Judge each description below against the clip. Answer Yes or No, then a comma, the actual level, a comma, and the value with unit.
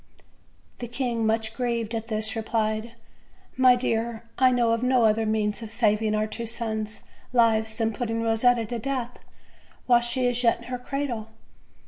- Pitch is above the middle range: Yes, high, 230 Hz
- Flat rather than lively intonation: Yes, narrow, 1.8 semitones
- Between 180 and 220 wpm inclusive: No, average, 170 wpm